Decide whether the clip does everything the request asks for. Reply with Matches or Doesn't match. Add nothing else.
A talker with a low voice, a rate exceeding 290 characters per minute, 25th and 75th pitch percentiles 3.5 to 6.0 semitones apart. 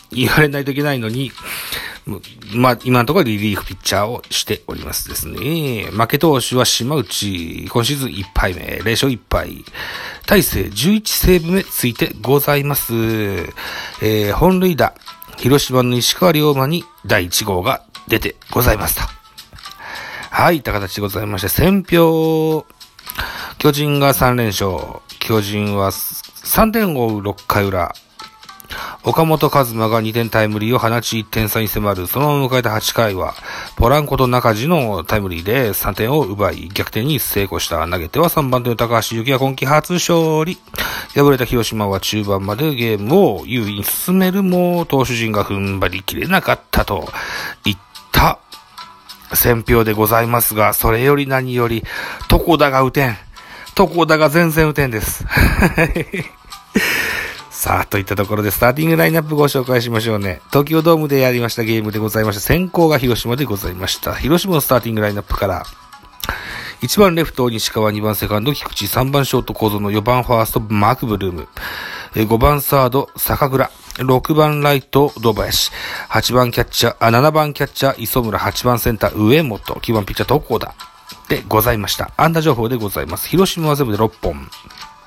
Matches